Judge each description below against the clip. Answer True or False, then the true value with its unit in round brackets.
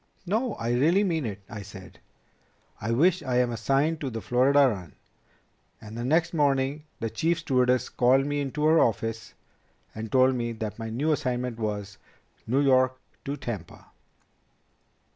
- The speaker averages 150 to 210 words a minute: True (160 wpm)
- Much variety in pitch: False (4.4 semitones)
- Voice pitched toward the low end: True (130 Hz)